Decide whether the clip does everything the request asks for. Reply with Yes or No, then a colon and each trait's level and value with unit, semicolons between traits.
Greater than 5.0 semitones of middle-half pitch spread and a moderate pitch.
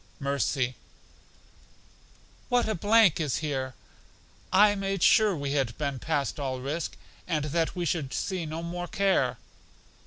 Yes: wide, 5.4 semitones; medium, 160 Hz